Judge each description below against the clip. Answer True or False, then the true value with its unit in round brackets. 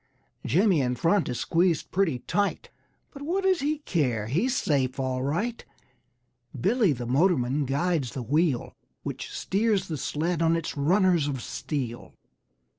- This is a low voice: False (165 Hz)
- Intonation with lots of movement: True (6.6 semitones)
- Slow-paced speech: False (145 wpm)